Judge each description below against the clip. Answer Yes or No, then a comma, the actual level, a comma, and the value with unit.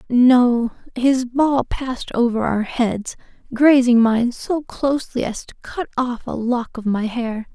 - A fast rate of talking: No, average, 160 wpm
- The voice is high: Yes, high, 245 Hz